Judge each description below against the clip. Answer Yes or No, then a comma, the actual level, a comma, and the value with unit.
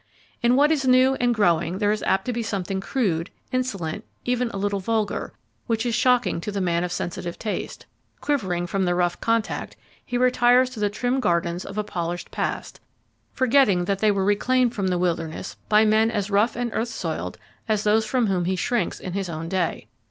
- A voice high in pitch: Yes, high, 210 Hz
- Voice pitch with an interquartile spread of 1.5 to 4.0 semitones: No, average, 5.1 semitones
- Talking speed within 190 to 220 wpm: Yes, average, 200 wpm